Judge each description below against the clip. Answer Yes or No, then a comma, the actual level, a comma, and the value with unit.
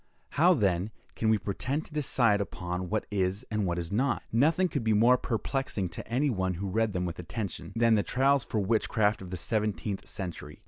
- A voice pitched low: Yes, low, 105 Hz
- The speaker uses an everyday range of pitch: Yes, average, 4.7 semitones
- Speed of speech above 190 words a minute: Yes, average, 200 wpm